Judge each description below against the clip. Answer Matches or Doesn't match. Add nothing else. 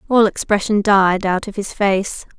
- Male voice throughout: Doesn't match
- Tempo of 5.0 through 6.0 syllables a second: Doesn't match